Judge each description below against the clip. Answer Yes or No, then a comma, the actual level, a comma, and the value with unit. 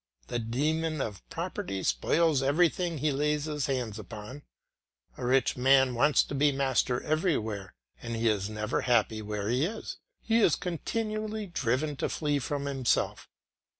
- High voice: No, low, 135 Hz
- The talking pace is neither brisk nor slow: Yes, average, 150 wpm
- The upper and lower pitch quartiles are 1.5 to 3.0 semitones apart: No, wide, 5.4 semitones